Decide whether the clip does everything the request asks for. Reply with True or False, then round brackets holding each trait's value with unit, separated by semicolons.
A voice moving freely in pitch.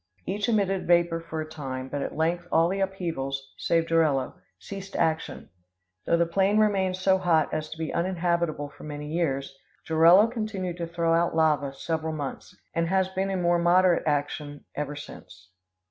False (3.5 semitones)